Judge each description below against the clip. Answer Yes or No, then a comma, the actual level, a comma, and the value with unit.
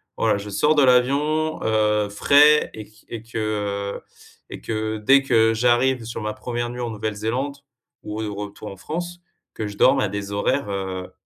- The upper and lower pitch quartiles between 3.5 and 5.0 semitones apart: Yes, average, 4.1 semitones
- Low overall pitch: Yes, low, 110 Hz